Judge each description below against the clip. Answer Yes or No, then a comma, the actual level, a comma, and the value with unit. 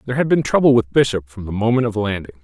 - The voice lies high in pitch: No, low, 110 Hz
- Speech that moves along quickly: Yes, fast, 270 wpm